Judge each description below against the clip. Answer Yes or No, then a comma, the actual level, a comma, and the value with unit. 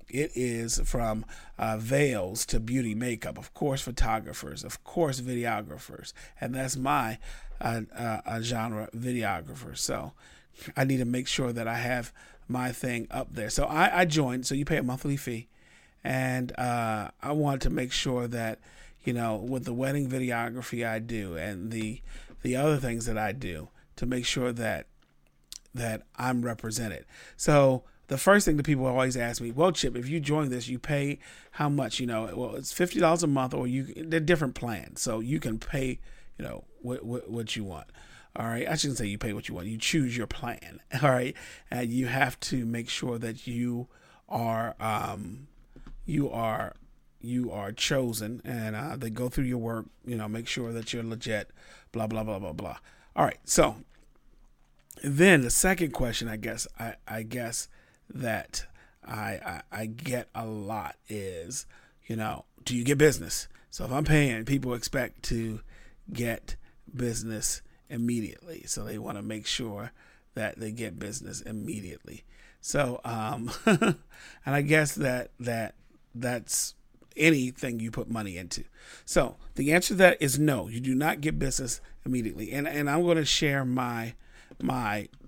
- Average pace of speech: Yes, average, 175 wpm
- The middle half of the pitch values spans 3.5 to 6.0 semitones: No, average, 3.1 semitones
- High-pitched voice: No, low, 120 Hz